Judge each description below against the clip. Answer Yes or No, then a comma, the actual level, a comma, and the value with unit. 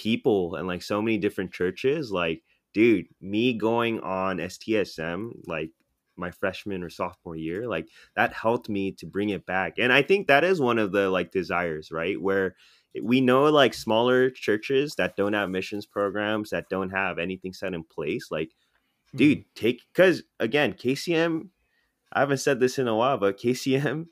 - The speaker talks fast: No, average, 175 wpm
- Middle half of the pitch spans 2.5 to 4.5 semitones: No, average, 5.2 semitones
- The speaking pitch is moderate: No, low, 105 Hz